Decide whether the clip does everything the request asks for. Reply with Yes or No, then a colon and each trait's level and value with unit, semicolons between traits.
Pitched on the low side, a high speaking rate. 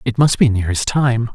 Yes: low, 115 Hz; fast, 265 wpm